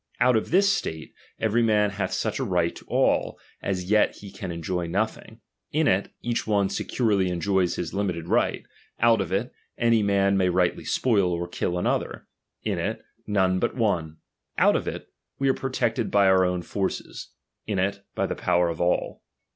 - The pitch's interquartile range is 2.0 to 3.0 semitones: No, average, 3.6 semitones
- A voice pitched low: Yes, low, 100 Hz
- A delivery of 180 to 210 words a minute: Yes, average, 185 wpm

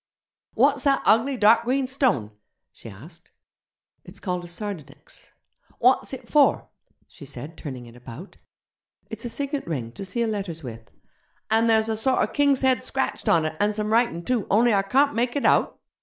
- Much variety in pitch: Yes, wide, 7.2 semitones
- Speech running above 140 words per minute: Yes, average, 175 wpm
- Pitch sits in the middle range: No, high, 215 Hz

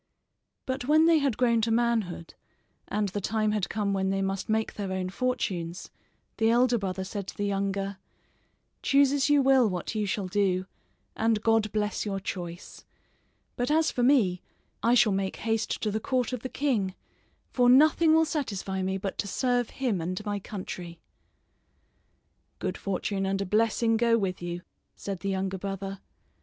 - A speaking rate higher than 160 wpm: Yes, average, 175 wpm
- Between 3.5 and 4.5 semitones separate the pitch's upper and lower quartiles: Yes, average, 4.1 semitones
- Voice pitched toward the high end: Yes, high, 210 Hz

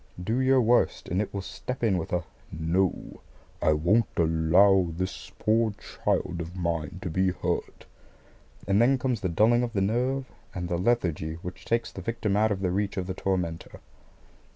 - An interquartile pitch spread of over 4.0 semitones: Yes, average, 4.4 semitones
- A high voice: No, very low, 95 Hz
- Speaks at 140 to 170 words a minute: No, average, 180 wpm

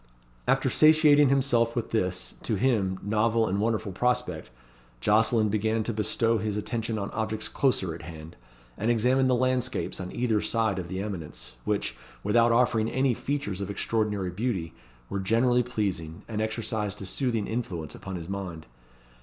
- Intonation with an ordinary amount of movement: Yes, average, 3.7 semitones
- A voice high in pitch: No, low, 110 Hz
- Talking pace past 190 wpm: No, average, 160 wpm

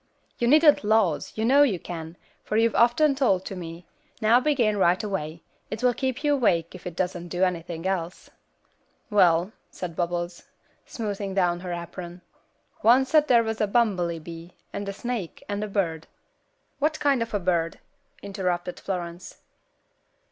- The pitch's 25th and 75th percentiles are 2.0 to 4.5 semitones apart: No, average, 4.9 semitones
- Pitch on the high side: Yes, high, 195 Hz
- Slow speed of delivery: No, average, 160 wpm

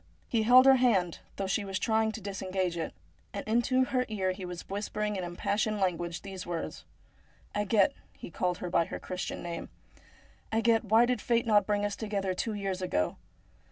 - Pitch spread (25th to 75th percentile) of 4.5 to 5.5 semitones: No, average, 3.2 semitones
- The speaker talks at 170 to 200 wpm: Yes, average, 190 wpm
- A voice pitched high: Yes, high, 200 Hz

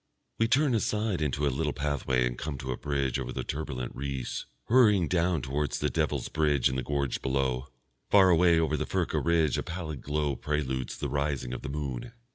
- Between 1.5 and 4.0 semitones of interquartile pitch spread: Yes, average, 3.6 semitones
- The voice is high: No, very low, 75 Hz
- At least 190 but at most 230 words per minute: Yes, average, 200 wpm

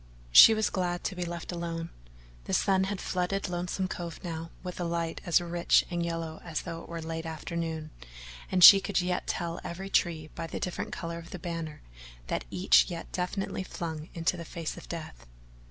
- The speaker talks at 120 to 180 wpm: No, average, 195 wpm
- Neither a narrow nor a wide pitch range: No, narrow, 1.5 semitones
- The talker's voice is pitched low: No, medium, 170 Hz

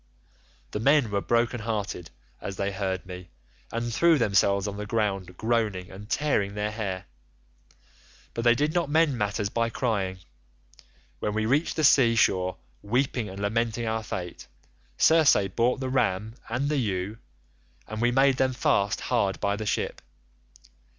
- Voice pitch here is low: Yes, low, 110 Hz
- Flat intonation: No, average, 3.7 semitones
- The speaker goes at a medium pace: Yes, average, 155 wpm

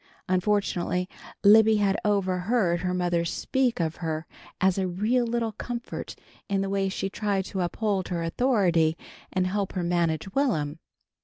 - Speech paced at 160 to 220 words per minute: No, average, 150 wpm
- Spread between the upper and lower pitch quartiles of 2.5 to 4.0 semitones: Yes, average, 3.2 semitones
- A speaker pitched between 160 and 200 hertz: Yes, high, 190 Hz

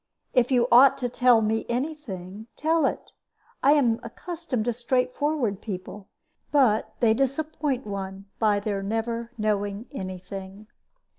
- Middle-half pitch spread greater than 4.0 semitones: Yes, average, 4.4 semitones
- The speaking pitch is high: Yes, high, 230 Hz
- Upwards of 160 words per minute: No, average, 140 wpm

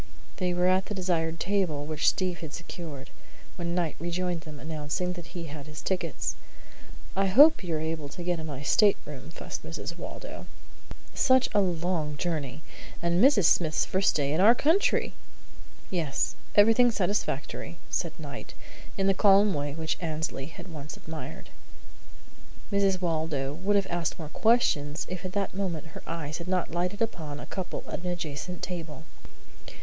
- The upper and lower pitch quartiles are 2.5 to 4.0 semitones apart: Yes, average, 3.3 semitones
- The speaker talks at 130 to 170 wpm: Yes, average, 165 wpm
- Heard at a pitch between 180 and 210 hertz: No, medium, 170 Hz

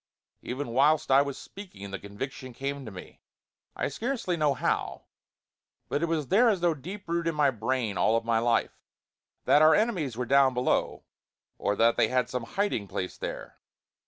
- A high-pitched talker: No, low, 135 Hz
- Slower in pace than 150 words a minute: No, average, 180 wpm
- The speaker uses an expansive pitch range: Yes, wide, 6.1 semitones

